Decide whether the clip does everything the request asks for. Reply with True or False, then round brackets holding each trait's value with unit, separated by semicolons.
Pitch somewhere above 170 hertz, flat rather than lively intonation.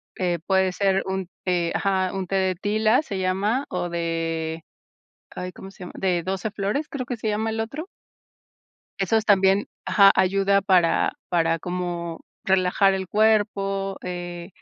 True (190 Hz; 2.3 semitones)